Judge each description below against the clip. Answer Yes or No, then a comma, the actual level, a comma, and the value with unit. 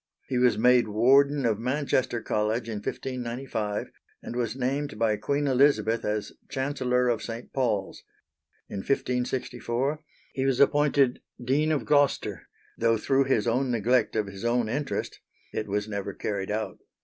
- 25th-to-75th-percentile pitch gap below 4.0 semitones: Yes, average, 3.6 semitones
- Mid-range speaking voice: No, low, 125 Hz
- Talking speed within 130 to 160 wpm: Yes, average, 150 wpm